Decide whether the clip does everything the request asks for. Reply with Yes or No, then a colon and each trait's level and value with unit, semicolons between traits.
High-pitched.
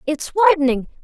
Yes: very high, 295 Hz